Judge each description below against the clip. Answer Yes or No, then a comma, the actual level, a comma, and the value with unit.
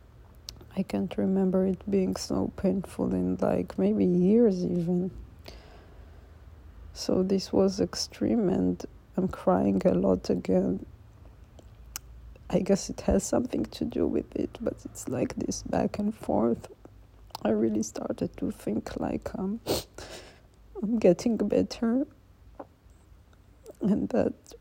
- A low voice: Yes, low, 110 Hz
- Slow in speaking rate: Yes, slow, 120 wpm